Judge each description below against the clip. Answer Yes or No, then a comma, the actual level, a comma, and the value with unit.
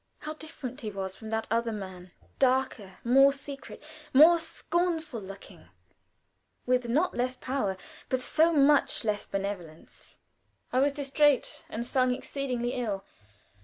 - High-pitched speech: Yes, very high, 255 Hz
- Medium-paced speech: No, slow, 130 wpm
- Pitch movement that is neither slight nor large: Yes, average, 4.7 semitones